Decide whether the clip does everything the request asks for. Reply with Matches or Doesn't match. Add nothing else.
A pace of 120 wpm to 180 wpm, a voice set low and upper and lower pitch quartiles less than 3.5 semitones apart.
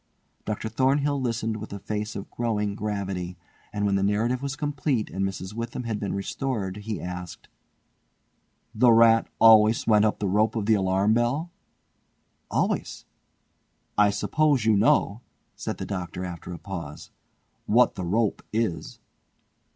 Matches